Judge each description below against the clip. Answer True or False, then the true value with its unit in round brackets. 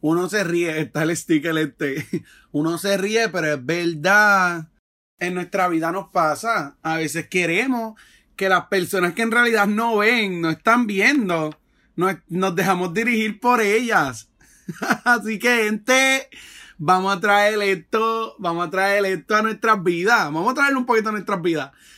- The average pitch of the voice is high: True (195 Hz)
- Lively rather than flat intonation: False (4.6 semitones)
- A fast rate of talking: False (165 wpm)